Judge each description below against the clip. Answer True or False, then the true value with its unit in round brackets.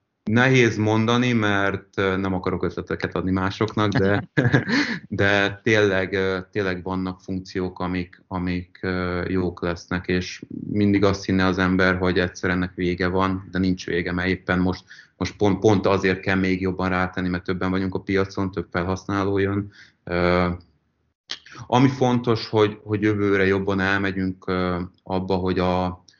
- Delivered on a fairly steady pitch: True (1.5 semitones)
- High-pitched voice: False (95 Hz)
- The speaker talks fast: False (140 wpm)